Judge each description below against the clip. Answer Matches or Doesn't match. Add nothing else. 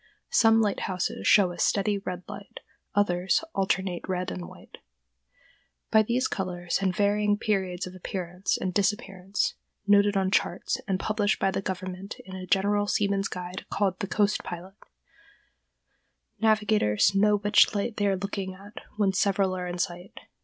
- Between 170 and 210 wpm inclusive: Doesn't match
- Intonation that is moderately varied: Doesn't match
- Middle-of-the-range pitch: Doesn't match